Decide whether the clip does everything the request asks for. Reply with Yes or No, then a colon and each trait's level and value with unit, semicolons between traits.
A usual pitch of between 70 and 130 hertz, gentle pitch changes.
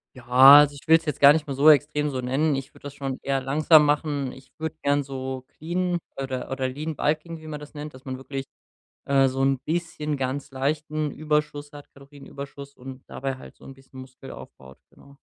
No: medium, 140 Hz; narrow, 2.2 semitones